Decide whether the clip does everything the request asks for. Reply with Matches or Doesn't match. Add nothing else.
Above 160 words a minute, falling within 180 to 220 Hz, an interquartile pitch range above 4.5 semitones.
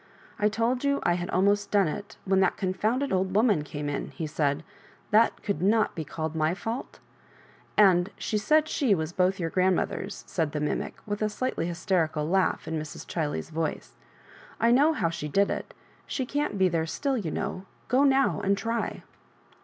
Matches